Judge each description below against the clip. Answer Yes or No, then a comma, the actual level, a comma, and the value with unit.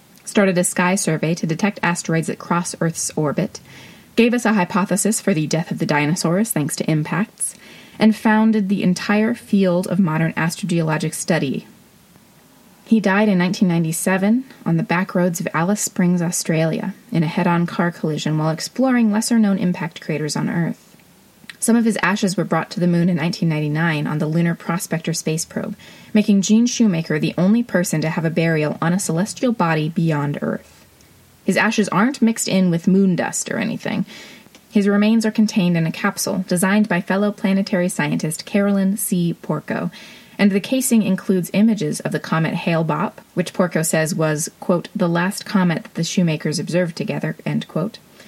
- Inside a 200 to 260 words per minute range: No, average, 175 wpm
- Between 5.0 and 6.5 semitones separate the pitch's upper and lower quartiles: No, average, 3.8 semitones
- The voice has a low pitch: No, medium, 185 Hz